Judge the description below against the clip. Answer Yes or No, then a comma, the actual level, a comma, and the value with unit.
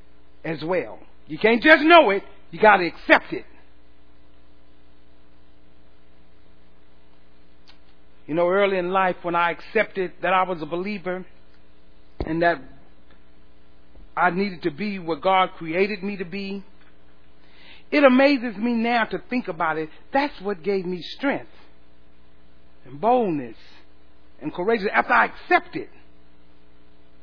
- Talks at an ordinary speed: No, slow, 130 wpm